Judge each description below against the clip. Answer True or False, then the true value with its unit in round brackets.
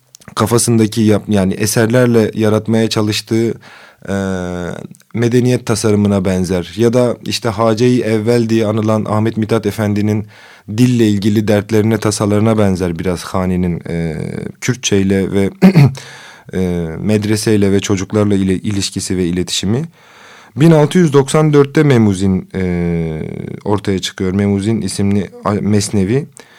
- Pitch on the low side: True (105 Hz)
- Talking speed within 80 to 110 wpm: True (105 wpm)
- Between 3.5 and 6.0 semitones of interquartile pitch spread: False (3.0 semitones)